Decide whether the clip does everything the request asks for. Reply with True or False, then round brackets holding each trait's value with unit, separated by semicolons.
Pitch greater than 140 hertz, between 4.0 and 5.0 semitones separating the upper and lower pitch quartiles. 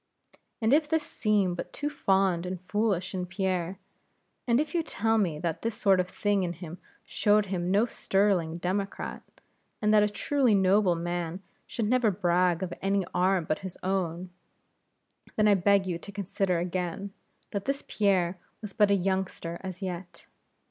False (190 Hz; 2.7 semitones)